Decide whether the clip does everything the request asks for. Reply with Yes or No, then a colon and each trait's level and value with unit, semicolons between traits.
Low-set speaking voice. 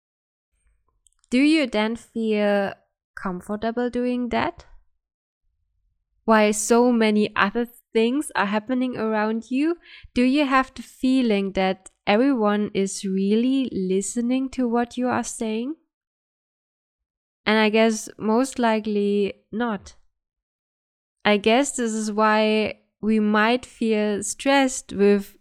No: high, 220 Hz